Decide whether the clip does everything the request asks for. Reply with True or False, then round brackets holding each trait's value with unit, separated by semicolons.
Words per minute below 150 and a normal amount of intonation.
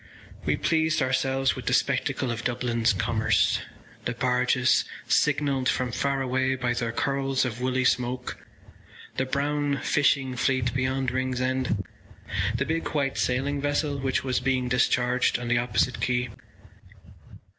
False (135 wpm; 1.5 semitones)